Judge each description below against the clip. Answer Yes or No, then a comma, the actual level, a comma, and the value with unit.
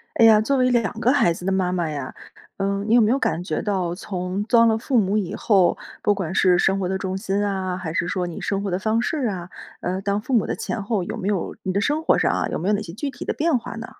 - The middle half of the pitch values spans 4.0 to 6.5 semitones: No, average, 3.4 semitones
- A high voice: Yes, high, 200 Hz